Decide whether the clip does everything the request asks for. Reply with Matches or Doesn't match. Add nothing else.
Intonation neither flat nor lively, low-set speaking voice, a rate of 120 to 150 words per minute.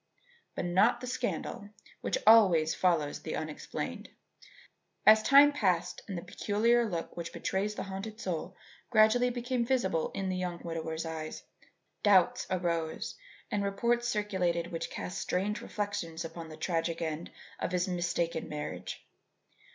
Doesn't match